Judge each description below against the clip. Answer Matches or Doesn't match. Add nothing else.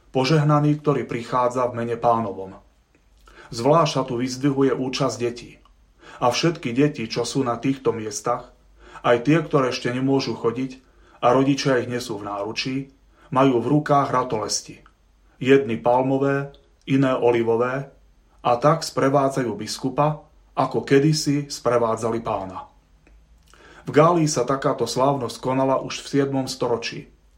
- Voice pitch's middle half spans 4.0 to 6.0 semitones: Doesn't match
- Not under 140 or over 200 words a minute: Doesn't match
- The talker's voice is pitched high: Doesn't match